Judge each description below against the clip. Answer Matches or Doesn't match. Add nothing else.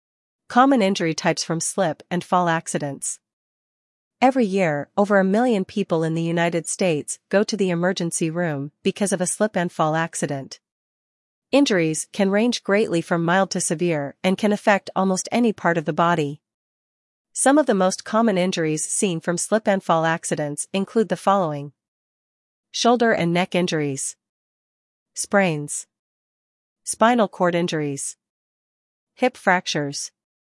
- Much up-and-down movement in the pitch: Doesn't match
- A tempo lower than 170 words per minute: Matches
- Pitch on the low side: Doesn't match